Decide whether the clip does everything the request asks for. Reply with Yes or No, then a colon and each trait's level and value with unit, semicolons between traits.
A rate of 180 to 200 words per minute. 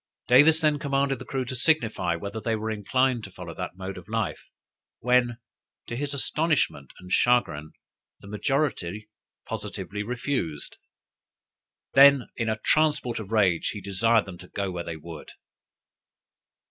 No: average, 145 wpm